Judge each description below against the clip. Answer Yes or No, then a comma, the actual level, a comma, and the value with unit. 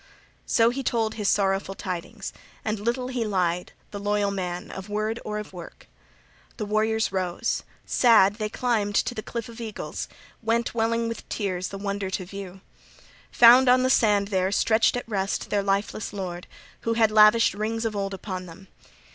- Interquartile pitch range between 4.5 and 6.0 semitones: No, average, 2.8 semitones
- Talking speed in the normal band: Yes, average, 180 wpm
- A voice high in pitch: Yes, high, 210 Hz